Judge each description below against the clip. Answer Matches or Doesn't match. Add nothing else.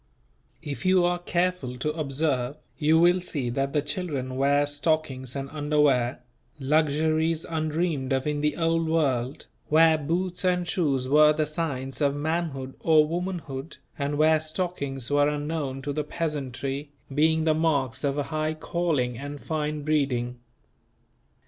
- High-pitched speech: Doesn't match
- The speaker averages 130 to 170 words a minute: Matches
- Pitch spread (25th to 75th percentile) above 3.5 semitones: Doesn't match